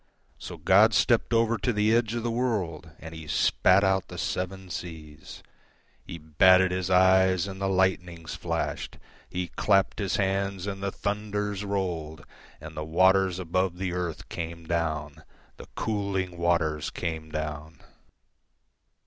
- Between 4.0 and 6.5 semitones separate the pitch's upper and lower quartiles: No, average, 3.1 semitones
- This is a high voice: No, very low, 95 Hz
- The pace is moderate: No, slow, 130 wpm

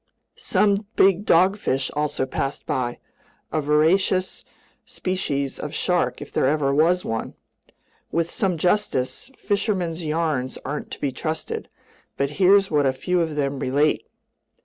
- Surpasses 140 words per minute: No, slow, 135 wpm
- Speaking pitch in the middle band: Yes, medium, 155 Hz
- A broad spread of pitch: No, average, 4.9 semitones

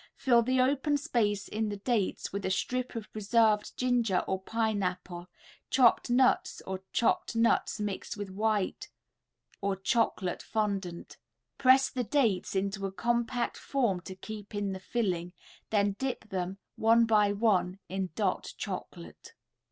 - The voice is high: Yes, high, 210 Hz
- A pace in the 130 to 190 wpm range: Yes, average, 145 wpm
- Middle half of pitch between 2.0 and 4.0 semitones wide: Yes, average, 3.7 semitones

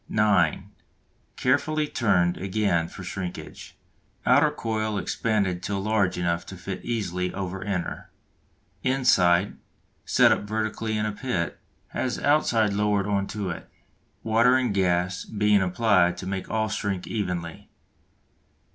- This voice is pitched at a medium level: No, low, 100 Hz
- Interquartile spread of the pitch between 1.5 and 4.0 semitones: Yes, average, 3.3 semitones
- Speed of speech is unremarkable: No, slow, 130 wpm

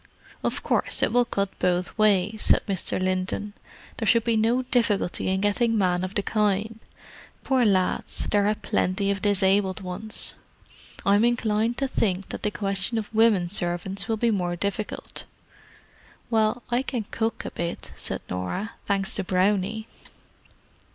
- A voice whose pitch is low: No, high, 205 Hz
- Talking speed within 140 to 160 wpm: Yes, average, 150 wpm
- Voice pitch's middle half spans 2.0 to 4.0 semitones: Yes, average, 2.9 semitones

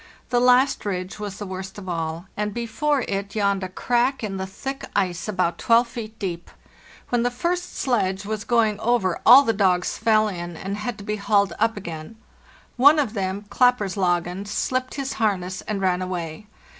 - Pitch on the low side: No, high, 205 Hz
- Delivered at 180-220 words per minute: Yes, average, 185 wpm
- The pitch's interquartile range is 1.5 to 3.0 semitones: No, average, 4.2 semitones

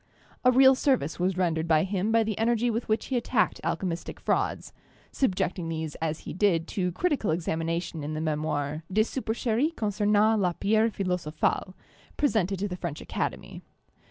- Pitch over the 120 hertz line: Yes, high, 190 Hz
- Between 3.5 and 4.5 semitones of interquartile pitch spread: No, average, 5.2 semitones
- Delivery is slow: No, average, 165 wpm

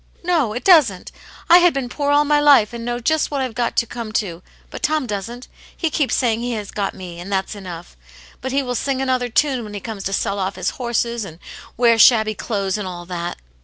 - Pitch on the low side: No, high, 235 Hz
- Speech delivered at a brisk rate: Yes, fast, 235 wpm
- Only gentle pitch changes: No, average, 4.9 semitones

